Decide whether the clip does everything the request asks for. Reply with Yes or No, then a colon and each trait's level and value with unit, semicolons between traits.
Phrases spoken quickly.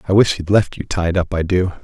Yes: fast, 295 wpm